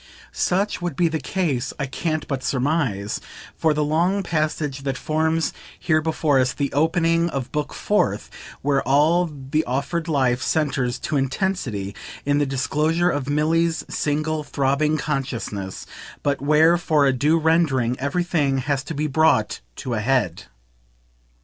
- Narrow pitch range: No, average, 3.2 semitones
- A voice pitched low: No, medium, 150 Hz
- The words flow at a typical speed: Yes, average, 150 wpm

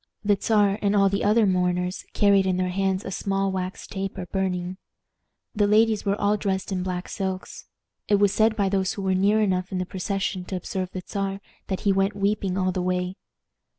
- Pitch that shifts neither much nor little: No, narrow, 1.5 semitones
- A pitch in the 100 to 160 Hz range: No, high, 195 Hz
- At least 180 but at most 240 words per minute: Yes, fast, 205 wpm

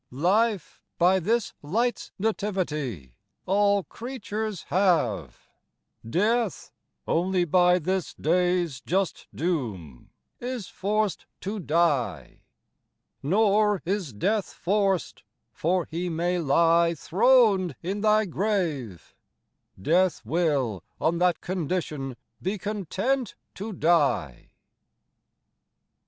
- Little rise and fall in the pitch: No, average, 4.4 semitones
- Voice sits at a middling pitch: Yes, medium, 180 Hz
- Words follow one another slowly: Yes, slow, 95 wpm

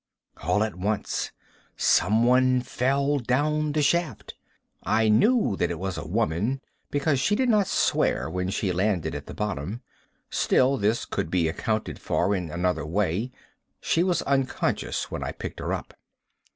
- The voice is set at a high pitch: No, low, 110 Hz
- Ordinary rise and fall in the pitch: No, wide, 6.9 semitones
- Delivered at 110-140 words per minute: No, average, 155 wpm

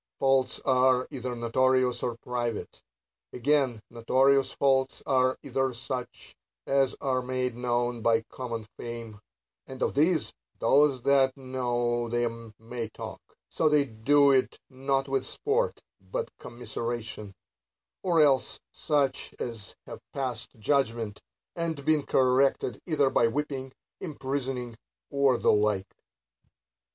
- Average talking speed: No, slow, 120 wpm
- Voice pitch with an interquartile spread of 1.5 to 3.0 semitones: Yes, narrow, 2.6 semitones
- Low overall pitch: Yes, low, 130 Hz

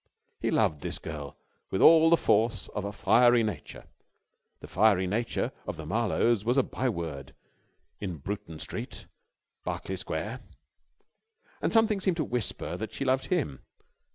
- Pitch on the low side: Yes, low, 110 Hz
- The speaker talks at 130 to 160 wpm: Yes, average, 150 wpm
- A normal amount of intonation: No, wide, 6.2 semitones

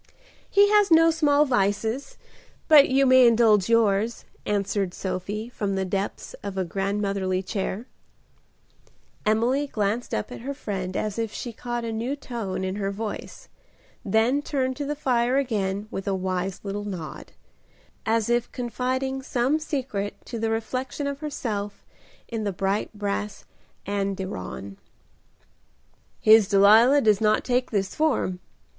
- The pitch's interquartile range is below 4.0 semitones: No, average, 4.6 semitones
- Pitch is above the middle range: Yes, high, 220 Hz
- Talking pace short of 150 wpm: Yes, average, 140 wpm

